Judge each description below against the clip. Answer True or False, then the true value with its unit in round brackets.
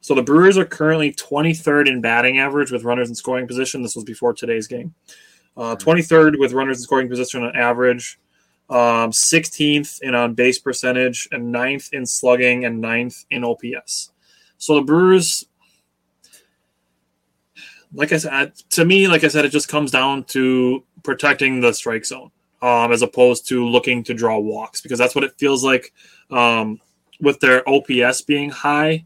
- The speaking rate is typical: True (170 wpm)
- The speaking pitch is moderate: False (125 Hz)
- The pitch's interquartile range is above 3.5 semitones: False (3.2 semitones)